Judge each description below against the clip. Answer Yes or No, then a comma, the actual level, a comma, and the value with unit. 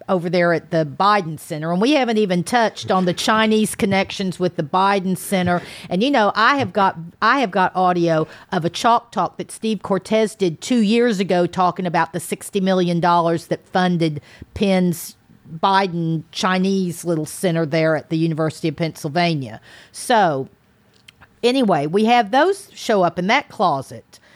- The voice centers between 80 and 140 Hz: No, medium, 185 Hz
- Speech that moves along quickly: No, average, 170 wpm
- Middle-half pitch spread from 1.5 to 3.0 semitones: No, average, 3.6 semitones